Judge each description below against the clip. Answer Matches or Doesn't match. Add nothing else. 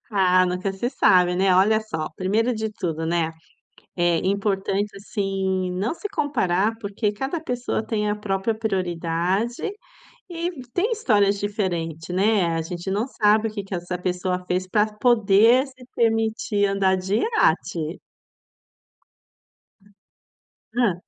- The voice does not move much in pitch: Doesn't match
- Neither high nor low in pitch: Doesn't match